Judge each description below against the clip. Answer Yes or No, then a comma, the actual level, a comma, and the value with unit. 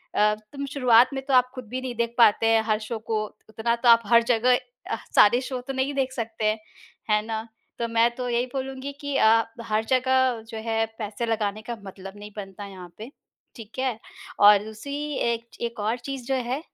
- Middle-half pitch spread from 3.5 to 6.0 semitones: No, average, 2.8 semitones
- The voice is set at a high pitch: Yes, high, 235 Hz